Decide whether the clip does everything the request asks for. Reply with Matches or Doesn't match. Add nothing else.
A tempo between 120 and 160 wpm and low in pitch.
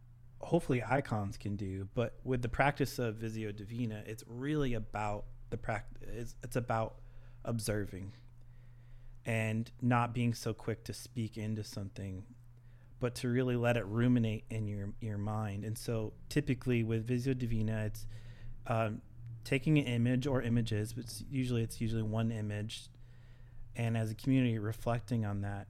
Matches